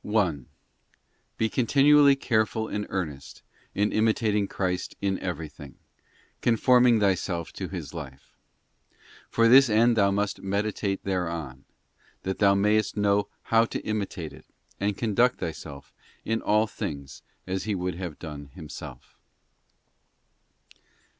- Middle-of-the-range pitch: No, low, 100 Hz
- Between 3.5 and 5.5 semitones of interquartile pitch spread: Yes, average, 4.5 semitones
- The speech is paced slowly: Yes, slow, 120 wpm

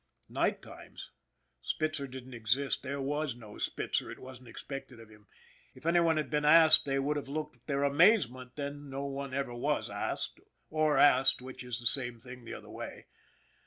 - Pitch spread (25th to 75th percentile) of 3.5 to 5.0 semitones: No, average, 2.9 semitones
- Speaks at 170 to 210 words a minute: Yes, average, 190 wpm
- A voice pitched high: No, low, 135 Hz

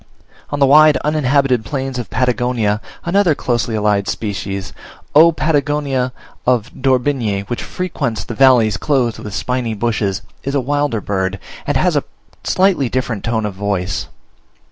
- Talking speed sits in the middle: Yes, average, 145 wpm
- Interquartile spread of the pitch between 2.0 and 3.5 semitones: No, average, 5.0 semitones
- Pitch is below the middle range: Yes, low, 125 Hz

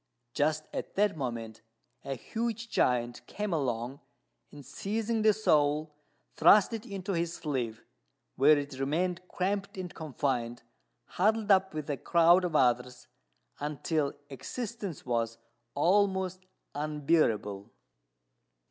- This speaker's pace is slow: Yes, slow, 115 wpm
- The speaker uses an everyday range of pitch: No, wide, 6.5 semitones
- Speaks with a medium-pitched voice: Yes, medium, 155 Hz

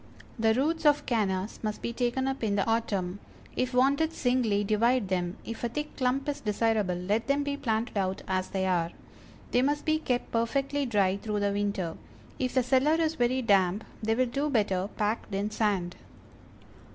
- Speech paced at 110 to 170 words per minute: No, average, 185 wpm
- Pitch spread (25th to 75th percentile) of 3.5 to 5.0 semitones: Yes, average, 4.6 semitones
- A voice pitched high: Yes, high, 225 Hz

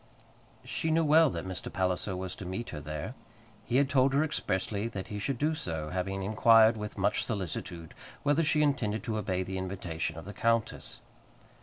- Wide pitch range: Yes, wide, 5.7 semitones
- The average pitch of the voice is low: Yes, low, 105 Hz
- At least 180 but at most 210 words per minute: Yes, average, 185 wpm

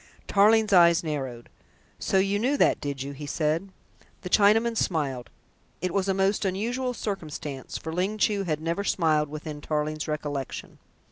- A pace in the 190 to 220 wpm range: No, average, 155 wpm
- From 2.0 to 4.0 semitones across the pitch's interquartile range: No, average, 4.9 semitones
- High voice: No, medium, 170 Hz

